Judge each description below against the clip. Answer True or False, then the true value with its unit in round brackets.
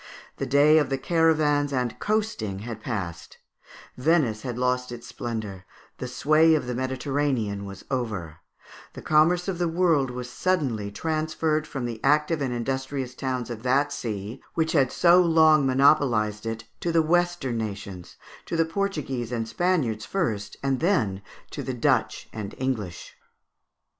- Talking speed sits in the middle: True (150 wpm)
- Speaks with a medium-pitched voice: False (130 Hz)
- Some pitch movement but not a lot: False (5.8 semitones)